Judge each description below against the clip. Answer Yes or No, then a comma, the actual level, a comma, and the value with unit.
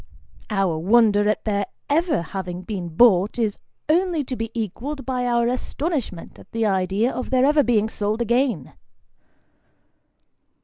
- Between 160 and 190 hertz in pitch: No, high, 225 Hz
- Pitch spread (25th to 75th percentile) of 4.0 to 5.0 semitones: Yes, average, 4.6 semitones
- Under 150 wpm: Yes, average, 140 wpm